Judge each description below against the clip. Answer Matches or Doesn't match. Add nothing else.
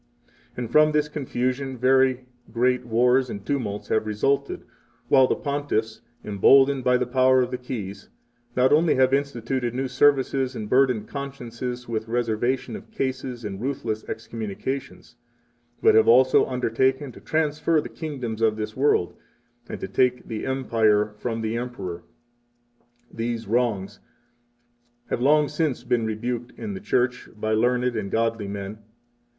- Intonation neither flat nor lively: Matches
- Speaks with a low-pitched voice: Matches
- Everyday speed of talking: Matches